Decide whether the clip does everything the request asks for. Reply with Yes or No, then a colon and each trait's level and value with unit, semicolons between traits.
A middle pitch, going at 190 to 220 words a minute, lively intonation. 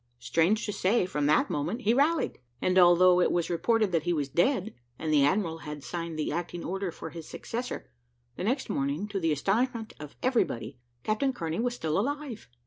Yes: medium, 180 Hz; average, 195 wpm; wide, 5.9 semitones